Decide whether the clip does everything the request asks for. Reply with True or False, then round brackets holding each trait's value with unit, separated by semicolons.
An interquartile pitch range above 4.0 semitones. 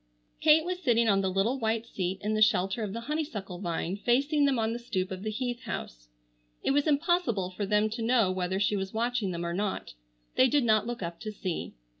True (4.4 semitones)